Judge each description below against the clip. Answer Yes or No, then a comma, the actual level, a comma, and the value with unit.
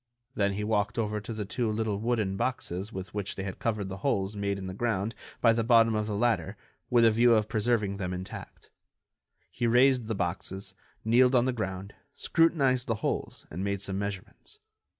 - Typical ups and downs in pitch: Yes, average, 3.0 semitones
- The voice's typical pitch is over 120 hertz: No, low, 105 Hz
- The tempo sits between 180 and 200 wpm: Yes, average, 195 wpm